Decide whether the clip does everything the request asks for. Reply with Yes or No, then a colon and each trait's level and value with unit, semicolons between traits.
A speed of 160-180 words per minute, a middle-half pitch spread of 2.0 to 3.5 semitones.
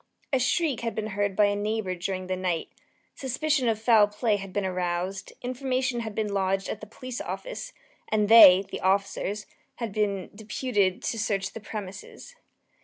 Yes: average, 175 wpm; average, 3.2 semitones